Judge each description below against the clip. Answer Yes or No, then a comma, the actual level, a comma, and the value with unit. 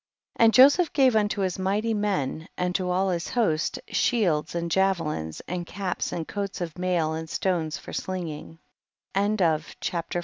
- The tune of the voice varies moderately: Yes, average, 3.6 semitones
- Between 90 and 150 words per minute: No, average, 175 wpm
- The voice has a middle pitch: Yes, medium, 180 Hz